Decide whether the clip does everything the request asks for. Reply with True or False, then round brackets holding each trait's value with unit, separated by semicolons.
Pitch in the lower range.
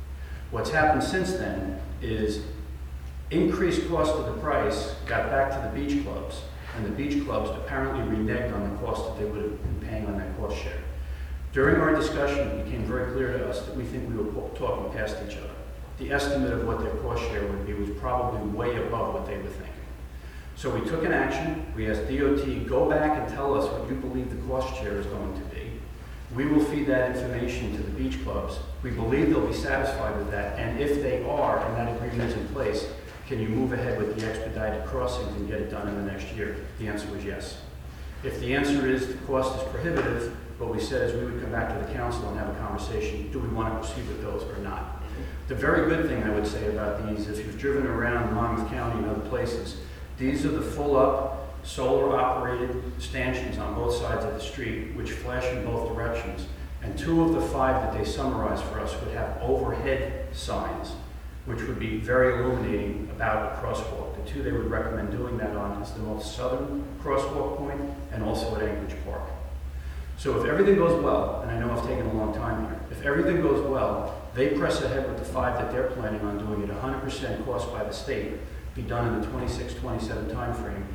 True (105 Hz)